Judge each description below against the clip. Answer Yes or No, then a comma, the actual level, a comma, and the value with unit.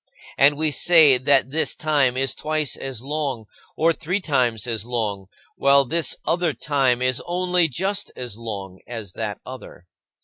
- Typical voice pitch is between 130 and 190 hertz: Yes, low, 135 Hz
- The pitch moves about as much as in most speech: Yes, average, 4.7 semitones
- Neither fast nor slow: Yes, average, 160 wpm